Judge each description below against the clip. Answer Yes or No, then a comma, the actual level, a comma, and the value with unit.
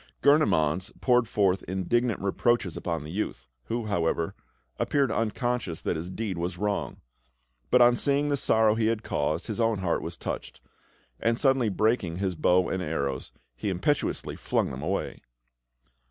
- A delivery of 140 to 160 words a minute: Yes, average, 155 wpm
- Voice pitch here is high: No, low, 100 Hz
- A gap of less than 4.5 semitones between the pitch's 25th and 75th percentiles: No, wide, 5.4 semitones